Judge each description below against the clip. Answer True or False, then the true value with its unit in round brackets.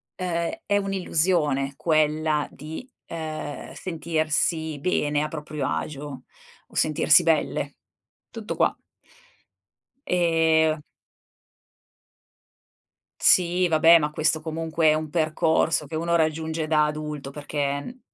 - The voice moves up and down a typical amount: False (1.7 semitones)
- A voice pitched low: False (155 Hz)